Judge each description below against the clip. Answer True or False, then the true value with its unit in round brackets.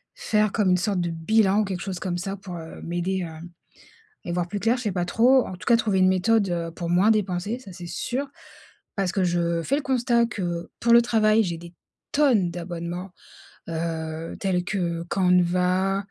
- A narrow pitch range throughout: False (3.6 semitones)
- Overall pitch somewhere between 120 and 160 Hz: False (185 Hz)